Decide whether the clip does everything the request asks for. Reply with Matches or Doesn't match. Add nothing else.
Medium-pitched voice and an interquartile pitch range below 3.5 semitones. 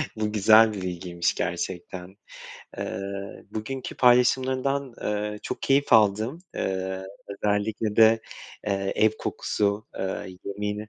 Doesn't match